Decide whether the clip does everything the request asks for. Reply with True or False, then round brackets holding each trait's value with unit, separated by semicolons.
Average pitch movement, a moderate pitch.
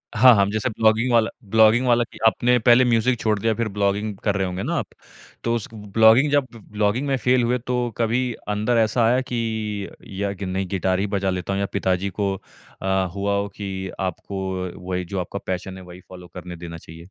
False (3.4 semitones; 105 Hz)